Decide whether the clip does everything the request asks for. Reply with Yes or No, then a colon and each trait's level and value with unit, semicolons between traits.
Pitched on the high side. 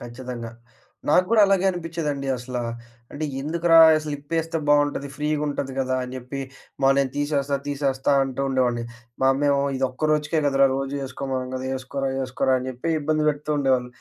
No: medium, 140 Hz